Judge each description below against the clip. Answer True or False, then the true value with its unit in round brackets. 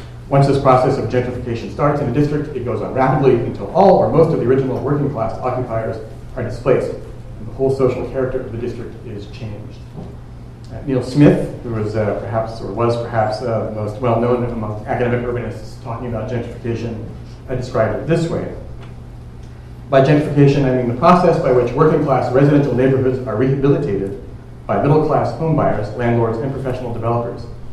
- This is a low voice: True (120 Hz)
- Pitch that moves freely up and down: False (3.0 semitones)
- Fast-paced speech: False (170 wpm)